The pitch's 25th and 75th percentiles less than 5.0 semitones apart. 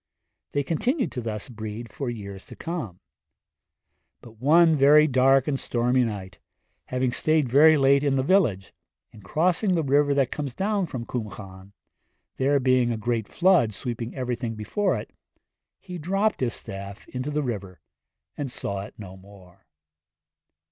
No: wide, 5.5 semitones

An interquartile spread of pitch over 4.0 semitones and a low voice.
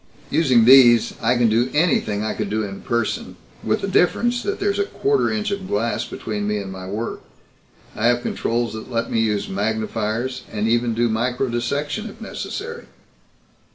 Yes: average, 4.8 semitones; low, 120 Hz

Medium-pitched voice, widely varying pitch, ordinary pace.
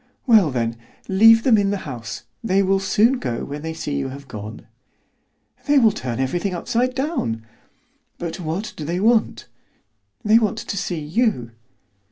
Yes: medium, 180 Hz; wide, 8.5 semitones; average, 165 wpm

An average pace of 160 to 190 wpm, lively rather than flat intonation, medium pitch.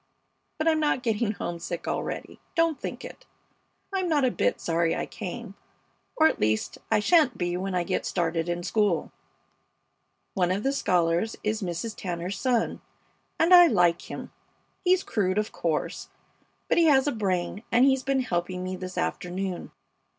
No: average, 165 wpm; wide, 7.2 semitones; high, 200 Hz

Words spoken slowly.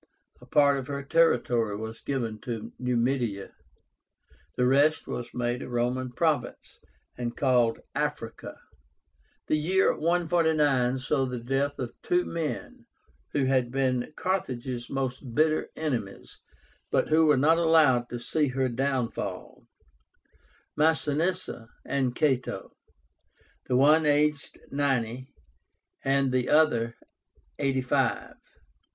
Yes: slow, 115 wpm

